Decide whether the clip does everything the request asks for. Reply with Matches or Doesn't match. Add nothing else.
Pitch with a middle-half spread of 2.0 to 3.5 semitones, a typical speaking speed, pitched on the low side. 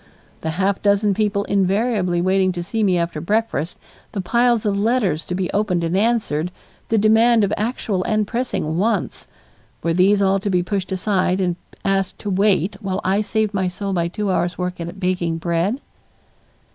Doesn't match